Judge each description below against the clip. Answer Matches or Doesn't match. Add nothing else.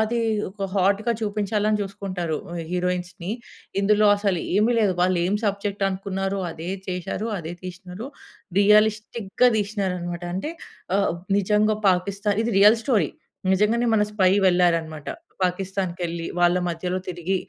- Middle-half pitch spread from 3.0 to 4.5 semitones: Doesn't match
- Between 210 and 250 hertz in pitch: Doesn't match